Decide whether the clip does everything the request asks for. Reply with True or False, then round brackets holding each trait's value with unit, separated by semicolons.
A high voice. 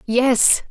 True (245 Hz)